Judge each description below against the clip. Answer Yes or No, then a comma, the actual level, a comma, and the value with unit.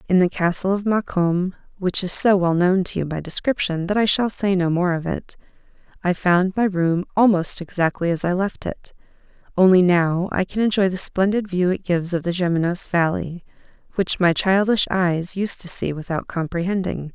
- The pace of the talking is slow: No, average, 195 wpm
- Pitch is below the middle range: No, medium, 180 Hz